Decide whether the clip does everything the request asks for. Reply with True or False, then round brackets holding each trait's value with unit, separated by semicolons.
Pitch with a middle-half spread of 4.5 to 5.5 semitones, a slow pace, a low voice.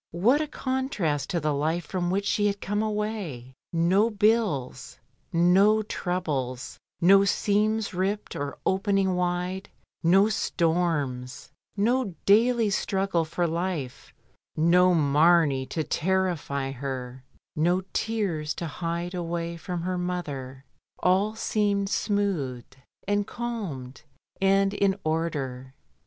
False (4.8 semitones; 115 wpm; 180 Hz)